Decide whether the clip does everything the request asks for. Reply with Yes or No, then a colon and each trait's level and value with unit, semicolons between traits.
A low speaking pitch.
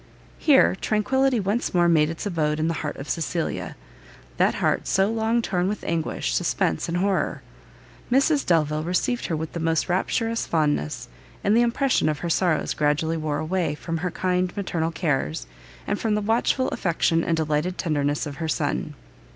No: medium, 170 Hz